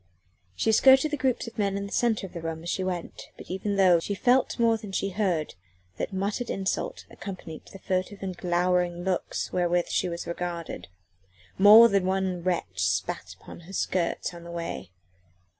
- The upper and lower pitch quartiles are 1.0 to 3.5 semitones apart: Yes, average, 2.8 semitones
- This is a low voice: No, medium, 185 Hz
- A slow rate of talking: No, average, 185 wpm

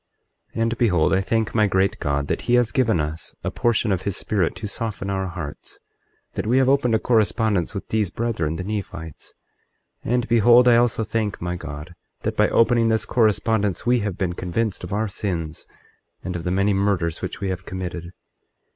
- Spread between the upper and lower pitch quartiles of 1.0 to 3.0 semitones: No, average, 4.3 semitones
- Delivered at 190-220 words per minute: Yes, average, 200 wpm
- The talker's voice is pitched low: Yes, low, 100 Hz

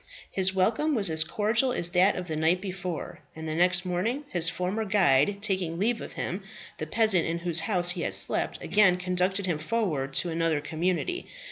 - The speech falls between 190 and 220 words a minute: Yes, average, 195 wpm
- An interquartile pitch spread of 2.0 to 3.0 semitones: No, average, 3.5 semitones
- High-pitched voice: No, medium, 180 Hz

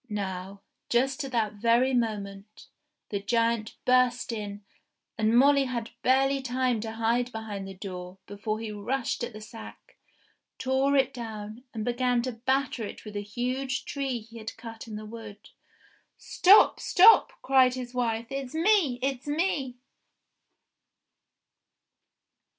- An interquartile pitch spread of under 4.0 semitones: Yes, average, 3.4 semitones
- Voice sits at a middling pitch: No, high, 235 Hz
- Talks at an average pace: Yes, average, 145 wpm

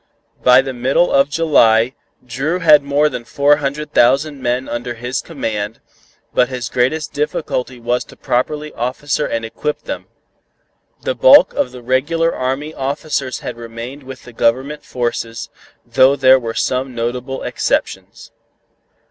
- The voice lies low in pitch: Yes, low, 130 Hz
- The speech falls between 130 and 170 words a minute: Yes, average, 145 wpm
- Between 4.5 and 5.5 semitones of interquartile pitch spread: No, average, 3.2 semitones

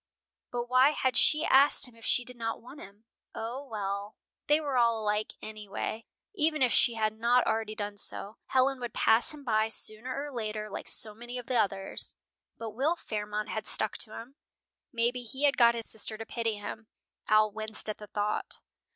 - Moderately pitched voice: No, high, 225 Hz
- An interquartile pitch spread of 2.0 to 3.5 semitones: Yes, average, 2.8 semitones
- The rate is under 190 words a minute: No, average, 195 wpm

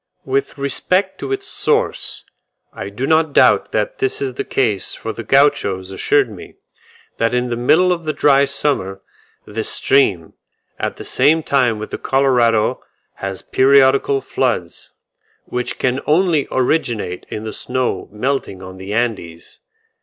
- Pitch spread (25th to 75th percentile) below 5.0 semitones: No, average, 5.3 semitones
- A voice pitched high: No, low, 130 Hz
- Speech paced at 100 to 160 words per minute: Yes, average, 150 wpm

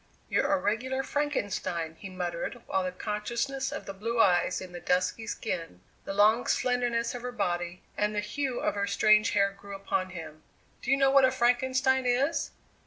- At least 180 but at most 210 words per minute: Yes, average, 185 wpm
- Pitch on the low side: No, high, 215 Hz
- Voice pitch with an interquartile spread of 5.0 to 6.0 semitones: Yes, wide, 5.4 semitones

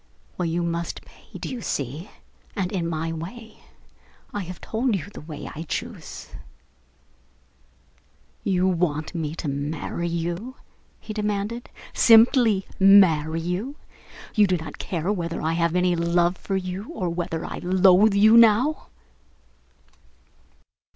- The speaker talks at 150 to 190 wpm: No, slow, 135 wpm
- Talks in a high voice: No, medium, 180 Hz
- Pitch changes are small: No, average, 3.7 semitones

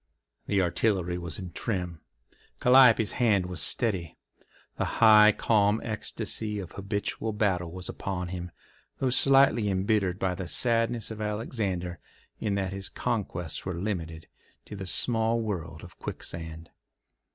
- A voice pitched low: Yes, low, 100 Hz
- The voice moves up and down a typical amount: Yes, average, 3.8 semitones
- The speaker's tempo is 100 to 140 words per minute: Yes, slow, 135 wpm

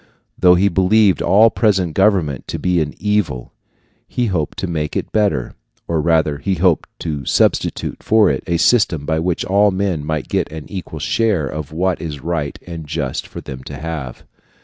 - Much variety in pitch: No, average, 4.3 semitones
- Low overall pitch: Yes, very low, 85 Hz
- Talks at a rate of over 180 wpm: Yes, average, 190 wpm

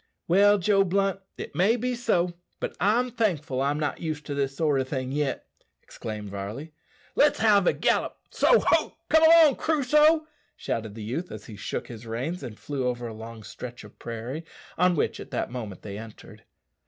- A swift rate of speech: No, average, 190 wpm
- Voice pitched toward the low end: No, medium, 150 Hz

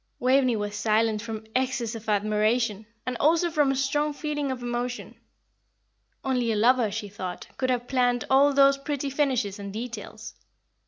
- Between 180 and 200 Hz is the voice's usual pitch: No, high, 245 Hz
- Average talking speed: Yes, average, 160 wpm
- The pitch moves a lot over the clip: No, average, 3.9 semitones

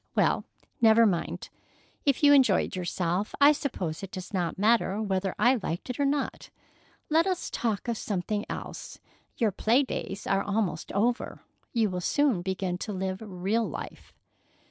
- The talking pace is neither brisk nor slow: Yes, average, 160 wpm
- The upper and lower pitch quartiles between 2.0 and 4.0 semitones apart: No, average, 4.4 semitones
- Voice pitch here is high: Yes, high, 210 Hz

